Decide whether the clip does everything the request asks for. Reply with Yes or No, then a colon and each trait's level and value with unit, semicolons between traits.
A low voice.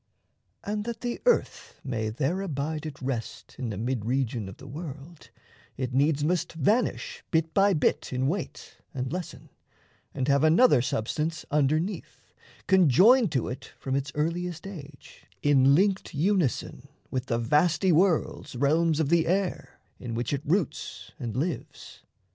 No: medium, 150 Hz